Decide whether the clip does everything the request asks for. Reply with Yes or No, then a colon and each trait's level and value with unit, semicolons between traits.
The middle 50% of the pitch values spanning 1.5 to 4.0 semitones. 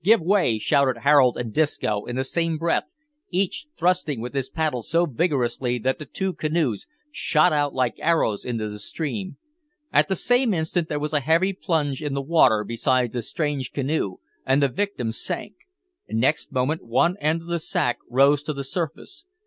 No: average, 4.9 semitones